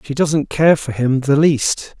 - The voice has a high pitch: No, medium, 145 Hz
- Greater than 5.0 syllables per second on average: No, 3.7 syllables/s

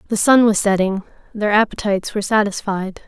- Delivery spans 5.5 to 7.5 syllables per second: Yes, 5.9 syllables/s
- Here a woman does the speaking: Yes, female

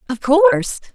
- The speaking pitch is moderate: No, very high, 300 Hz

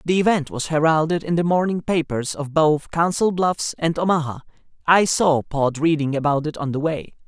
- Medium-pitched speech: Yes, medium, 160 Hz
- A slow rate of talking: No, average, 190 wpm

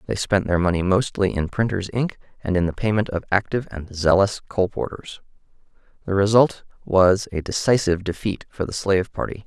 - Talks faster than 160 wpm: Yes, average, 170 wpm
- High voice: No, low, 100 Hz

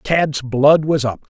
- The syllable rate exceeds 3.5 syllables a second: No, 3.2 syllables/s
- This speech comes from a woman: No, male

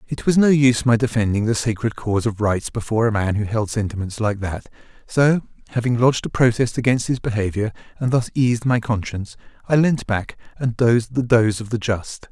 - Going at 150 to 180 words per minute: No, fast, 205 wpm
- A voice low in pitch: Yes, low, 115 Hz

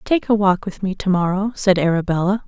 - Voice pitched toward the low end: No, high, 190 Hz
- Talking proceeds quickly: Yes, fast, 220 wpm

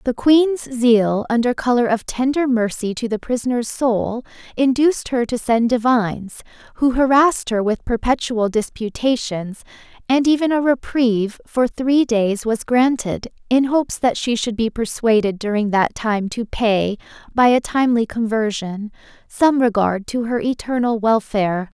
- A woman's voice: Yes, female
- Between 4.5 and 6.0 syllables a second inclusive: Yes, 4.6 syllables/s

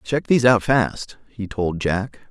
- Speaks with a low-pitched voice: Yes, low, 110 Hz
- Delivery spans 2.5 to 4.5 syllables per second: Yes, 4.0 syllables/s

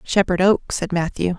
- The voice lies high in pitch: No, medium, 180 Hz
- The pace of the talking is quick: No, average, 175 wpm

